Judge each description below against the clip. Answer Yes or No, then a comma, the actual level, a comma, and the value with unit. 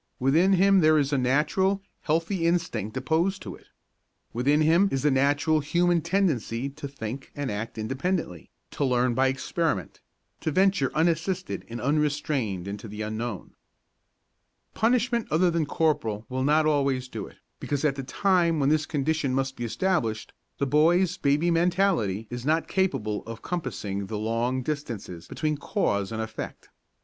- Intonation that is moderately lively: No, wide, 5.8 semitones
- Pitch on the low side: No, medium, 145 Hz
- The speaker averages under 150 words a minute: No, average, 155 wpm